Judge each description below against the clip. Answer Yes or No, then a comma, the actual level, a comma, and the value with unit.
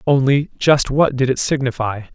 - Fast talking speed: No, average, 140 wpm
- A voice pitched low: Yes, low, 130 Hz